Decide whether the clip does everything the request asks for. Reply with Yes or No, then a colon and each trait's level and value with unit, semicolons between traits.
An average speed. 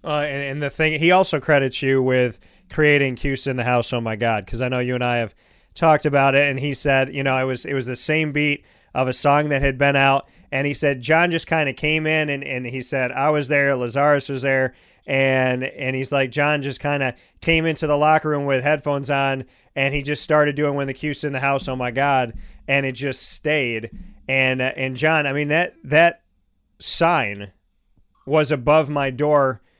No: fast, 230 wpm